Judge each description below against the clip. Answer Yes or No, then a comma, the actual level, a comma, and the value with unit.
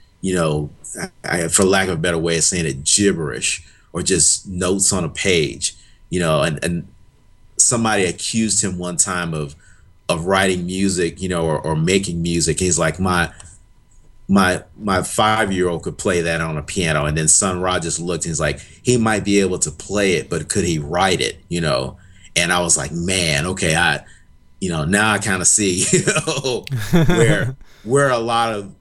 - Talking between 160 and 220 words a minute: Yes, average, 200 wpm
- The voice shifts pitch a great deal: No, average, 3.3 semitones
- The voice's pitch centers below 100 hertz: Yes, very low, 90 Hz